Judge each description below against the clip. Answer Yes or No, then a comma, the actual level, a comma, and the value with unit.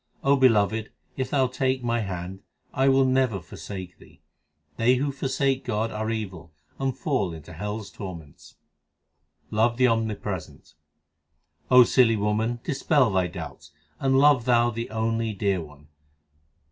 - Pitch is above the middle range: No, low, 115 Hz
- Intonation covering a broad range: No, average, 4.9 semitones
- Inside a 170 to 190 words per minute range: No, average, 145 wpm